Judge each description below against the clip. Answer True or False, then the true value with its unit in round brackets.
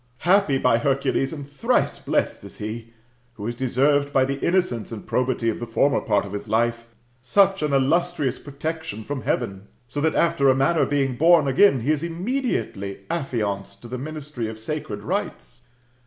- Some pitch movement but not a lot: True (5.0 semitones)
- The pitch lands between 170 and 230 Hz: False (135 Hz)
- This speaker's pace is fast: False (175 wpm)